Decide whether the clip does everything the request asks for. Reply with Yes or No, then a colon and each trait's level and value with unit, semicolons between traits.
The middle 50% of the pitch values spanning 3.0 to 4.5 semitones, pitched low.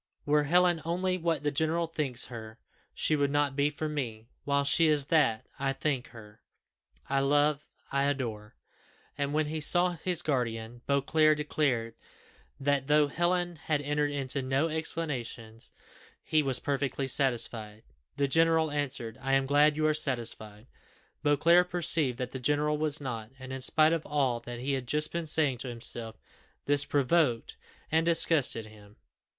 No: average, 3.5 semitones; medium, 145 Hz